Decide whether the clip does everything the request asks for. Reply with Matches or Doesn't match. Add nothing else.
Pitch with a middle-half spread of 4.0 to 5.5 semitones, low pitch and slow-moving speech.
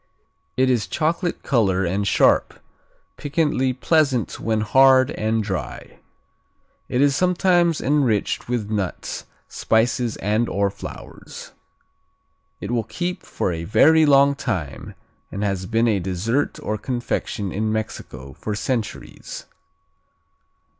Matches